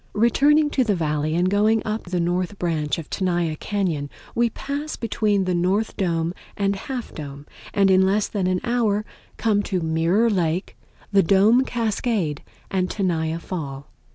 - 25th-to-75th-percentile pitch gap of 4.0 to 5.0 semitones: Yes, average, 4.3 semitones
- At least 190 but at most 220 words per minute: No, average, 160 wpm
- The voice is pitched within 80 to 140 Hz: No, high, 190 Hz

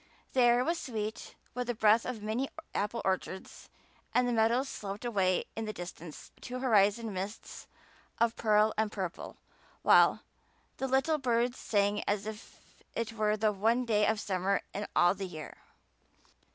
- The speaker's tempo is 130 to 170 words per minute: Yes, average, 160 wpm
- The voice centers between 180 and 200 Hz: No, high, 215 Hz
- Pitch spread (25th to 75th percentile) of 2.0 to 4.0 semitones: Yes, average, 3.1 semitones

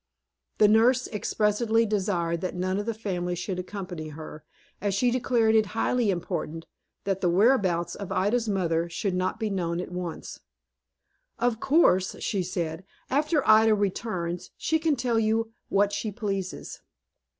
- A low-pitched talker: No, high, 200 Hz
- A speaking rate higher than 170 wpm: No, average, 150 wpm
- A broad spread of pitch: No, average, 3.9 semitones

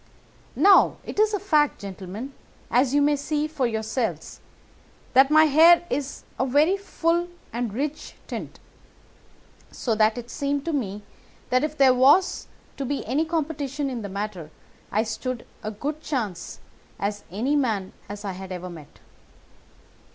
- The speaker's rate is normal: Yes, average, 160 wpm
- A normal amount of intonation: No, wide, 5.8 semitones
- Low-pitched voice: No, very high, 265 Hz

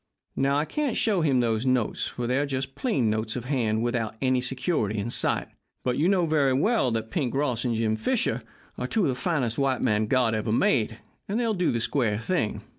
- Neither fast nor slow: No, fast, 215 wpm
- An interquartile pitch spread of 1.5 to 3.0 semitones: No, average, 4.4 semitones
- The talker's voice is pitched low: Yes, low, 130 Hz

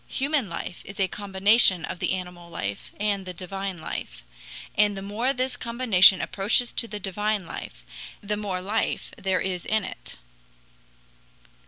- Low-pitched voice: No, high, 195 Hz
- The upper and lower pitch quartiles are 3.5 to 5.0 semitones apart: No, average, 2.7 semitones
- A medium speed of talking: Yes, average, 155 wpm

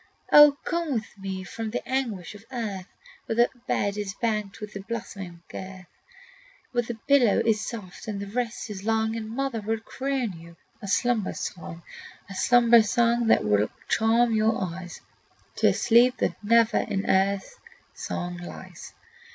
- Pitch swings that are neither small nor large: Yes, average, 3.5 semitones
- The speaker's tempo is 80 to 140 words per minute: No, average, 165 wpm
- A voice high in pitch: Yes, high, 220 Hz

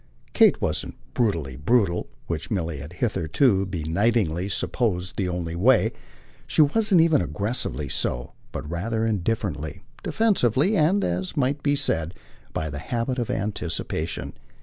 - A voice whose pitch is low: Yes, low, 100 Hz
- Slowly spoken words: Yes, slow, 130 wpm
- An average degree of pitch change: No, wide, 6.9 semitones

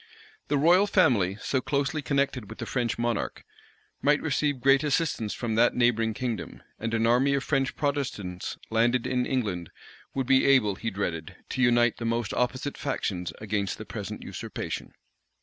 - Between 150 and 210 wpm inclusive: Yes, average, 165 wpm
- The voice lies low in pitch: Yes, low, 125 Hz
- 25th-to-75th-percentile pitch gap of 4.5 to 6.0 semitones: No, average, 3.7 semitones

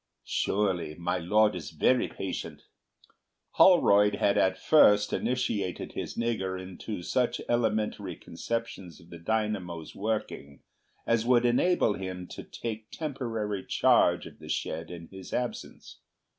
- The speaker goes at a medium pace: No, slow, 130 wpm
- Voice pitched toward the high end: No, low, 105 Hz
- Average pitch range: Yes, average, 4.2 semitones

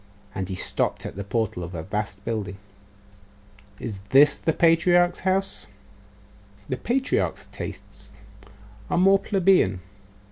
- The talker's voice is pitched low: Yes, low, 130 Hz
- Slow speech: Yes, slow, 120 wpm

